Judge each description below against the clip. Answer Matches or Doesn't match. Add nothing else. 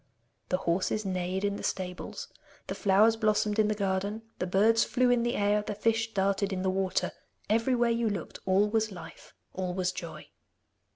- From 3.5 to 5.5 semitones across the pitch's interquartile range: Doesn't match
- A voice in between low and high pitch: Doesn't match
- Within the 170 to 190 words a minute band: Matches